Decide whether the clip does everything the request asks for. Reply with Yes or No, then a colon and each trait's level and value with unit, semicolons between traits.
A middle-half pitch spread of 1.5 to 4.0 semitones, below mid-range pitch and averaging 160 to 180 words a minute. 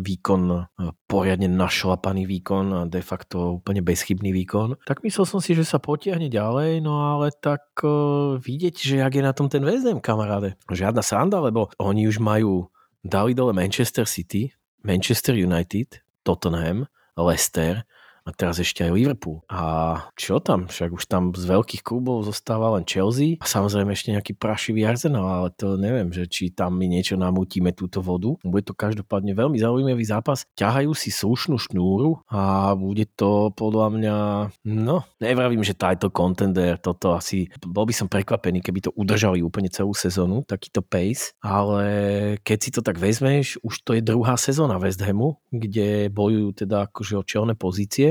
No: average, 4.4 semitones; low, 105 Hz; fast, 165 wpm